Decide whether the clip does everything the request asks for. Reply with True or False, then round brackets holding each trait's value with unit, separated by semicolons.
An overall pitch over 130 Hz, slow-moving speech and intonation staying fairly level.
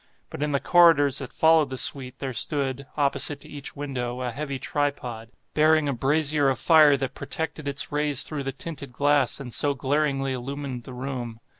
False (140 Hz; 185 wpm; 2.1 semitones)